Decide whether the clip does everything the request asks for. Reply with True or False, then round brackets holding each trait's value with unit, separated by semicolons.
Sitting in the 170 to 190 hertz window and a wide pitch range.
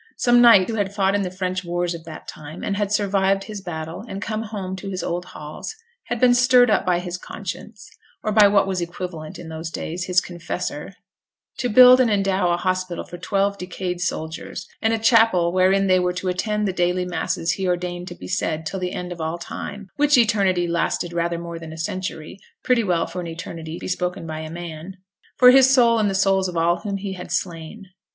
False (185 Hz; 2.8 semitones)